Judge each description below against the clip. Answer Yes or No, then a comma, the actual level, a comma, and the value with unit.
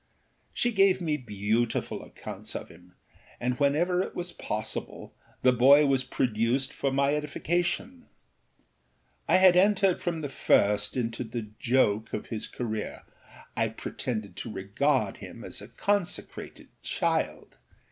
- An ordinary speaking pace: No, slow, 130 wpm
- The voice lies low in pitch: Yes, low, 130 Hz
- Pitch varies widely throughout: Yes, wide, 7.7 semitones